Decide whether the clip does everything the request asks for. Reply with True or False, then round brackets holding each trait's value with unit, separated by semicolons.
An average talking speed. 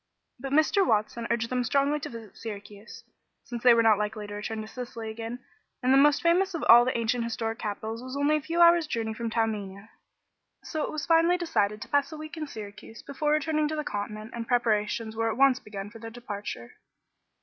False (215 wpm)